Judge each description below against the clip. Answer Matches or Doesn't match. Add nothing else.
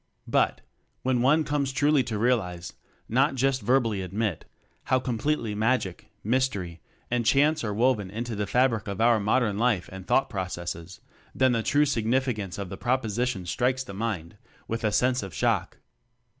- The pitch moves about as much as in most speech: Matches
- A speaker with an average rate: Matches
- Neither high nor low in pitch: Doesn't match